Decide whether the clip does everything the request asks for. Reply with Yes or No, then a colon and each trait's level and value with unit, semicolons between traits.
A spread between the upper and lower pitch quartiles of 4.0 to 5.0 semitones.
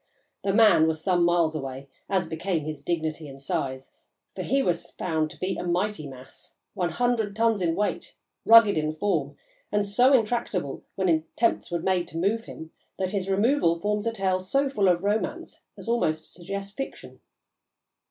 Yes: average, 4.6 semitones